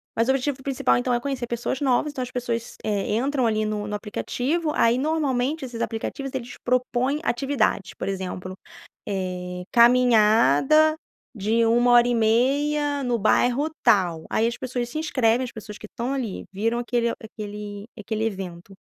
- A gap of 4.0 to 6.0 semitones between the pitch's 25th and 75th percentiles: No, average, 3.6 semitones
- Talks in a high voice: Yes, high, 235 Hz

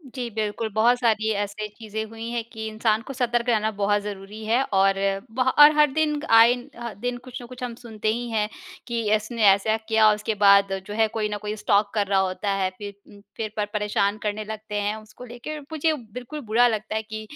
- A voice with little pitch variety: Yes, narrow, 2.3 semitones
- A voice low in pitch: No, high, 220 Hz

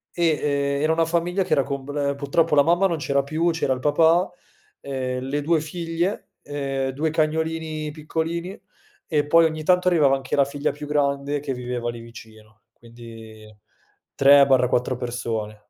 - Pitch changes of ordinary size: Yes, average, 3.5 semitones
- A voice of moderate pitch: Yes, medium, 145 Hz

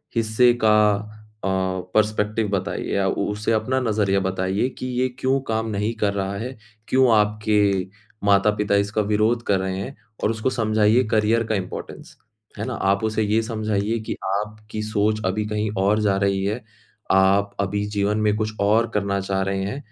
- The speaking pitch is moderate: No, low, 105 Hz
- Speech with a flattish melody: Yes, narrow, 1.6 semitones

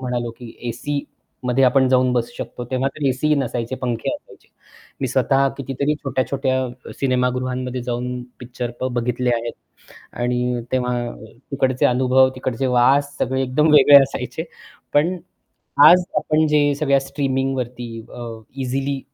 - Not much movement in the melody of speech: Yes, narrow, 1.8 semitones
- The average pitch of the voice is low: Yes, low, 130 Hz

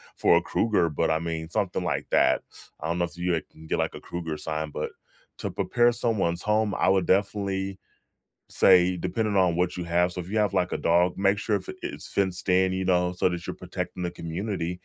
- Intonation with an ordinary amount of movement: No, narrow, 2.3 semitones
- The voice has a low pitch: Yes, very low, 90 Hz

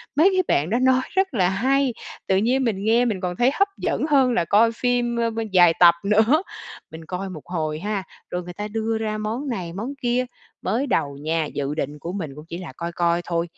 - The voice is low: No, high, 205 Hz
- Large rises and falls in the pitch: Yes, wide, 6.1 semitones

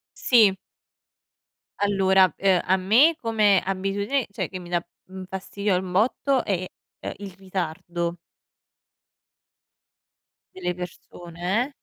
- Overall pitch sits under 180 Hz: No, high, 190 Hz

